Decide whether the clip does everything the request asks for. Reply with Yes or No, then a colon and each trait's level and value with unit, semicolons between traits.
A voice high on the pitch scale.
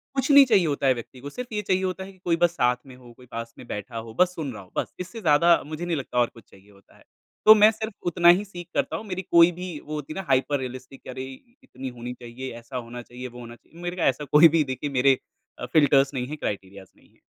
No: medium, 140 Hz